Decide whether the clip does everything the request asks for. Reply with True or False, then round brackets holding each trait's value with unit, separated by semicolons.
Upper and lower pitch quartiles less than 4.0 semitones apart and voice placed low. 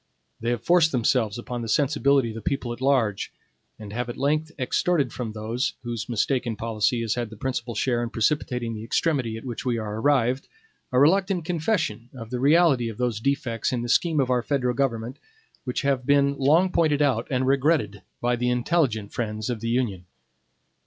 True (3.5 semitones; 125 Hz)